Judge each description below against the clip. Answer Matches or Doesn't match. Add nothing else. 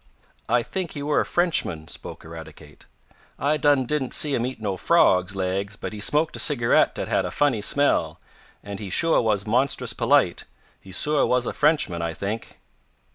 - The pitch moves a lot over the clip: Matches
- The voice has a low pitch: Matches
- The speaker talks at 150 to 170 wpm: Doesn't match